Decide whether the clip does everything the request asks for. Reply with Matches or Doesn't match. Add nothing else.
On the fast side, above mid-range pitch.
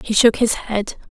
Matches